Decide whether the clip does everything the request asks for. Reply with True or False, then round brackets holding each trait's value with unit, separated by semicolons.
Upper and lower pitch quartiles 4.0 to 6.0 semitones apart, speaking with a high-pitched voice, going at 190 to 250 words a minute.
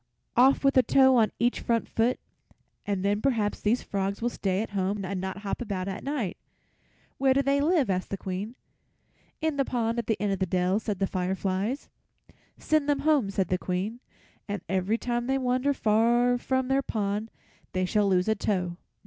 True (4.7 semitones; 215 Hz; 195 wpm)